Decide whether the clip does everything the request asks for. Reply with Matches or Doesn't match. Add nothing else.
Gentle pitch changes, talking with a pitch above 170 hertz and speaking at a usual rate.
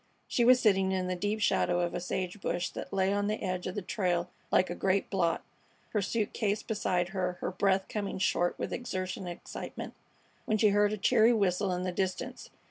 Doesn't match